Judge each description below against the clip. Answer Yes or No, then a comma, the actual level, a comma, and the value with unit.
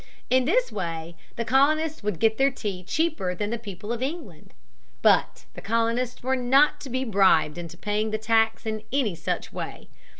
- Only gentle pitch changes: No, average, 4.9 semitones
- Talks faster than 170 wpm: Yes, average, 180 wpm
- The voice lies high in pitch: Yes, high, 225 Hz